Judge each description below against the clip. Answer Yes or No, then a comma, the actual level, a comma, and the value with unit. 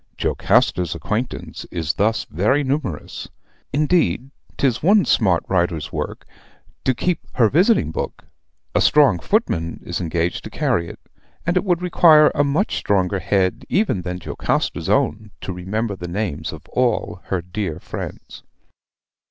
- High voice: No, low, 105 Hz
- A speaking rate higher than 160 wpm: No, average, 145 wpm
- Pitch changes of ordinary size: No, wide, 8.6 semitones